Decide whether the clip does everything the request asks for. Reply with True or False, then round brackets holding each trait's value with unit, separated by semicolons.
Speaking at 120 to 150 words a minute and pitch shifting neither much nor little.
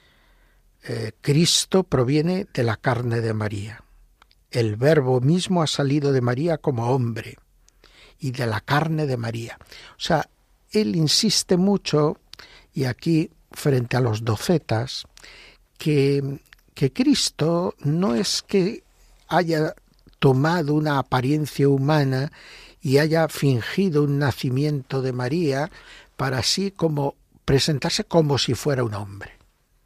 True (125 wpm; 4.3 semitones)